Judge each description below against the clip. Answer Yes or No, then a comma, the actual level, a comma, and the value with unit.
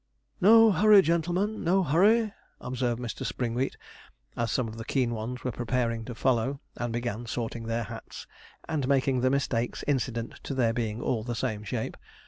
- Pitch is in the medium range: No, low, 125 Hz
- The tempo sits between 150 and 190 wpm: Yes, average, 170 wpm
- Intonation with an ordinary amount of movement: Yes, average, 3.8 semitones